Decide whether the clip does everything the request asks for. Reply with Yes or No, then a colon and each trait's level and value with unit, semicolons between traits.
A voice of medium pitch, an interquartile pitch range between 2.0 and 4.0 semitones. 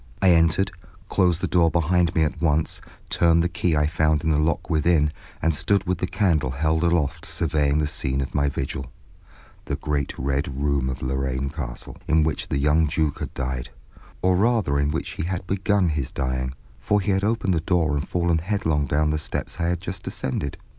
No: very low, 80 Hz; average, 3.6 semitones